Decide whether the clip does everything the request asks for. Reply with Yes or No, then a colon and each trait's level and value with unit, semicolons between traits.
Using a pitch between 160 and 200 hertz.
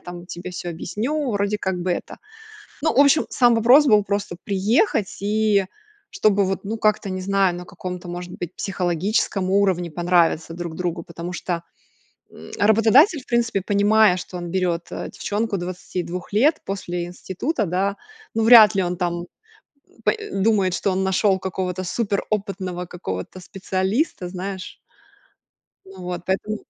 Yes: high, 190 Hz